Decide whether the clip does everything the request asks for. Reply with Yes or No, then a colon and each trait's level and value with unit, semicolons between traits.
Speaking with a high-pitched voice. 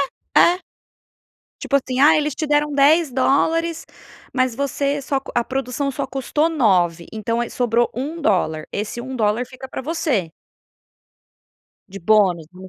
Yes: very high, 260 Hz